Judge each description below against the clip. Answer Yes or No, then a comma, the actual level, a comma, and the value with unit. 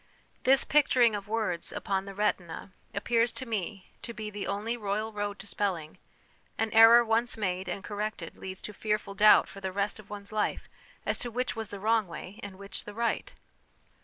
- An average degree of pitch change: No, narrow, 2.3 semitones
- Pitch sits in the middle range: No, high, 210 Hz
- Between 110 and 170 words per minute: No, average, 190 wpm